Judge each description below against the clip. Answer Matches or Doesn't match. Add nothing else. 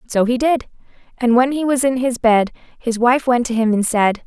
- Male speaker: Doesn't match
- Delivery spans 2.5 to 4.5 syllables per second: Doesn't match